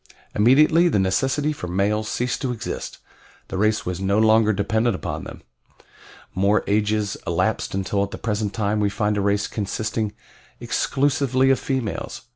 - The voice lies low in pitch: Yes, low, 105 Hz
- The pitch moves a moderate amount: Yes, average, 3.3 semitones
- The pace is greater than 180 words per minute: No, average, 155 wpm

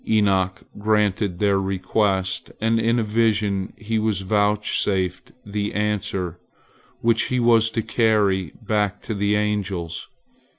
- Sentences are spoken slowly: Yes, slow, 125 wpm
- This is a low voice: Yes, low, 105 Hz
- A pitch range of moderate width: No, narrow, 2.2 semitones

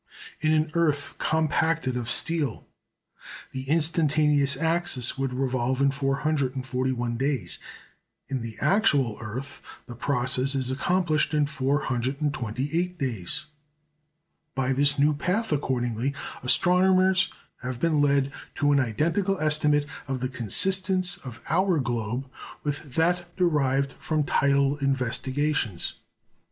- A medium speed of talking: No, slow, 115 wpm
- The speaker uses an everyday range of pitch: Yes, average, 3.4 semitones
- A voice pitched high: No, medium, 140 Hz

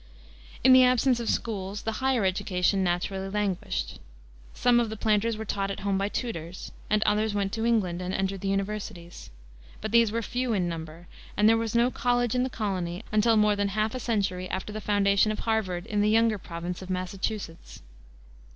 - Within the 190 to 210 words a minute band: Yes, average, 195 wpm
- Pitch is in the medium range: No, high, 205 Hz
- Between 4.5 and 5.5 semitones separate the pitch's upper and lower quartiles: No, average, 3.1 semitones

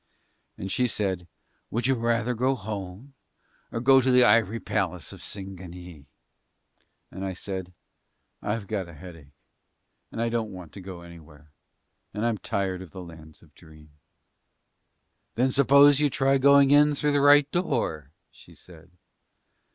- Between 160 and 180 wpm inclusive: No, average, 150 wpm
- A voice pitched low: Yes, low, 100 Hz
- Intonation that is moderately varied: No, wide, 6.3 semitones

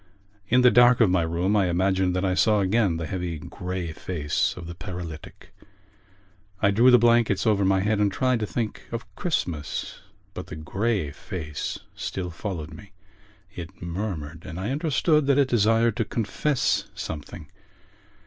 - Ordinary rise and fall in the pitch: Yes, average, 4.9 semitones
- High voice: No, very low, 95 Hz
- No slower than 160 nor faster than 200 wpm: Yes, average, 165 wpm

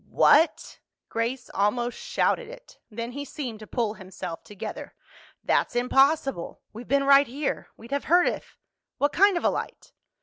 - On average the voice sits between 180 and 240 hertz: No, very high, 265 Hz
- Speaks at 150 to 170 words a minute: Yes, average, 155 wpm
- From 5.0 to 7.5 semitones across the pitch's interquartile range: No, average, 4.3 semitones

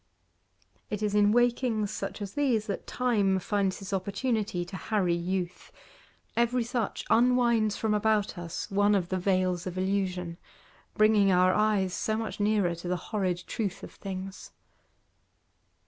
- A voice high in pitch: Yes, high, 200 Hz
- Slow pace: No, average, 145 wpm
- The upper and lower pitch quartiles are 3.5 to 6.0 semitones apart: No, average, 2.8 semitones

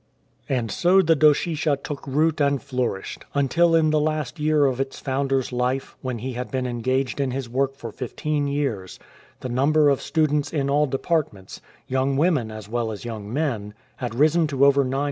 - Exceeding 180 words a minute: Yes, average, 190 wpm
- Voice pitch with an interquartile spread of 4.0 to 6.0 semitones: No, average, 3.3 semitones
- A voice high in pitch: No, low, 135 Hz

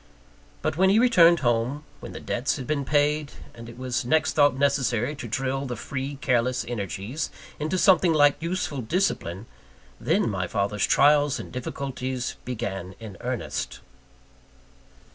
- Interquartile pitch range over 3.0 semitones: Yes, average, 4.0 semitones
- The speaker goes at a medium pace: Yes, average, 145 wpm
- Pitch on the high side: No, low, 130 Hz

